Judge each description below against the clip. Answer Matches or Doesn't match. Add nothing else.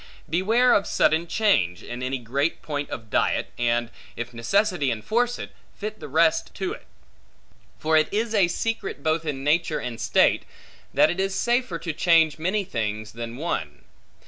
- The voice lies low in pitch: Doesn't match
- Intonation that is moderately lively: Doesn't match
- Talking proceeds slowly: Doesn't match